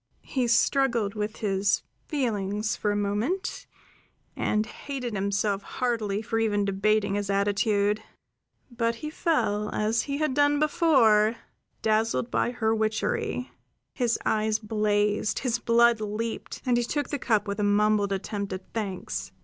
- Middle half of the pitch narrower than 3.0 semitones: Yes, narrow, 2.6 semitones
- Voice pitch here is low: No, high, 215 Hz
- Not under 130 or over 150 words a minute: Yes, average, 140 wpm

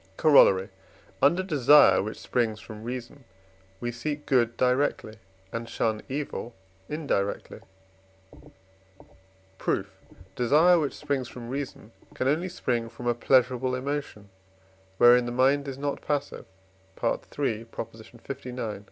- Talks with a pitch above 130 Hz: No, low, 125 Hz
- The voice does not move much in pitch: No, average, 3.5 semitones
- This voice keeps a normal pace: No, slow, 115 wpm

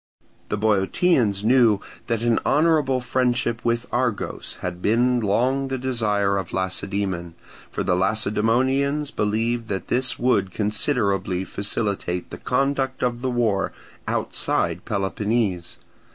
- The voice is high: No, low, 110 Hz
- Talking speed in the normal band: No, slow, 120 wpm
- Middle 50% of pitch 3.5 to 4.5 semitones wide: Yes, average, 4.2 semitones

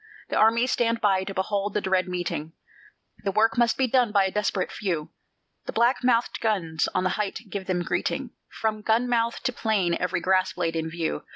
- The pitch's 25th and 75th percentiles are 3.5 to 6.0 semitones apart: Yes, average, 3.9 semitones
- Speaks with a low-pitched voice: No, high, 205 Hz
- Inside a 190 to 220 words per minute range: Yes, average, 200 wpm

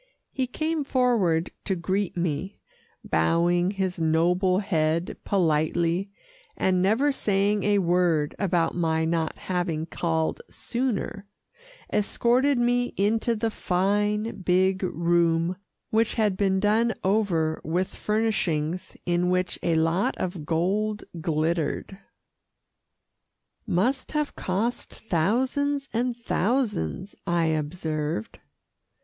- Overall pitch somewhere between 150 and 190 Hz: Yes, medium, 185 Hz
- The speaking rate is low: Yes, slow, 105 wpm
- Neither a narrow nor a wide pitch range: Yes, average, 4.2 semitones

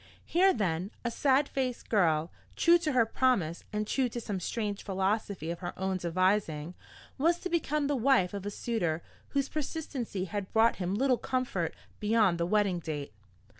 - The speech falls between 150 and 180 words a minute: Yes, average, 170 wpm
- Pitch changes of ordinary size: No, wide, 6.3 semitones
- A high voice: Yes, high, 210 Hz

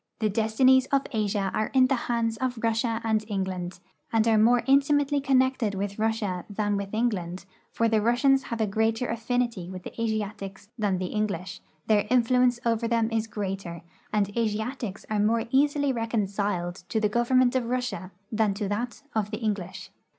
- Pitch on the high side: Yes, high, 220 Hz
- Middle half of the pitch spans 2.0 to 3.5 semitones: Yes, average, 3.1 semitones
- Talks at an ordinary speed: Yes, average, 175 wpm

